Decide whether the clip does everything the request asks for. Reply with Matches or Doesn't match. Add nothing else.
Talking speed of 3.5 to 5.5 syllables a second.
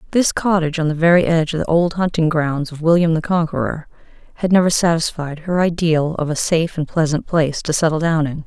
Doesn't match